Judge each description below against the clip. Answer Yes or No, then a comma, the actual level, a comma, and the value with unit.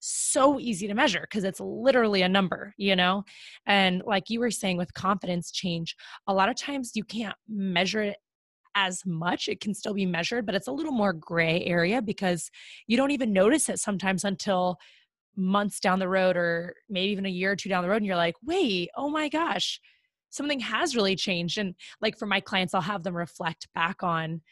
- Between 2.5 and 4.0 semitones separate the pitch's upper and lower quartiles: Yes, average, 3.1 semitones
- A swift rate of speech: Yes, fast, 210 wpm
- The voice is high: Yes, high, 195 Hz